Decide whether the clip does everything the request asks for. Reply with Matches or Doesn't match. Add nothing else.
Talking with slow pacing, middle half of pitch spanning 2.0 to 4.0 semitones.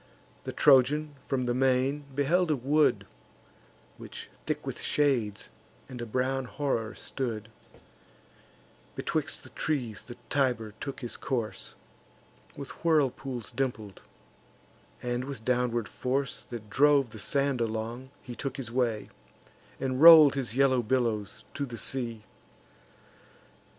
Matches